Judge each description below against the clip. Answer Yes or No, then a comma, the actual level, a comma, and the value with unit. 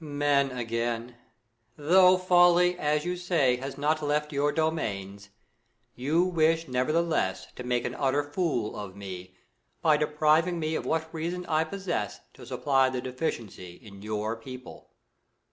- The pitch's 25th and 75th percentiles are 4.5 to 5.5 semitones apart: Yes, average, 5.2 semitones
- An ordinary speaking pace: Yes, average, 150 wpm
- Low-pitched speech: No, medium, 145 Hz